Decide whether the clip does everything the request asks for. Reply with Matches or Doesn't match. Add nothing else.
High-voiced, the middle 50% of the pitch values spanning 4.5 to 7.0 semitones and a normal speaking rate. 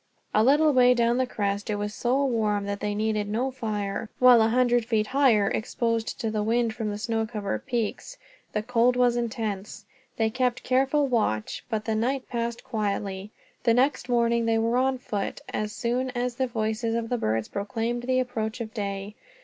Doesn't match